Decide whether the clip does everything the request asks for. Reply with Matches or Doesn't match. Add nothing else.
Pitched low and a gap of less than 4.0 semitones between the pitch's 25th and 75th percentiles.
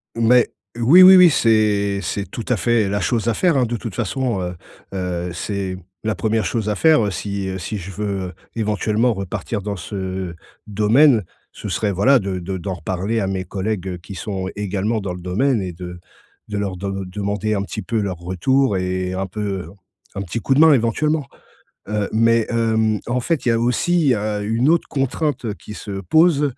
Matches